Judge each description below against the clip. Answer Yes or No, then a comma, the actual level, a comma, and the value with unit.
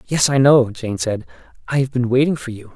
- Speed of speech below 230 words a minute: No, fast, 240 wpm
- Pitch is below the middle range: Yes, low, 120 Hz